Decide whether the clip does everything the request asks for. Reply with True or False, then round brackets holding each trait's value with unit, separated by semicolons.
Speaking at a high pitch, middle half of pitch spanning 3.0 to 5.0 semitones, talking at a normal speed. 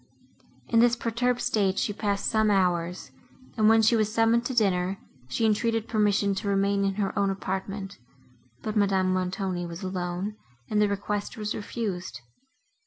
False (200 Hz; 2.4 semitones; 160 wpm)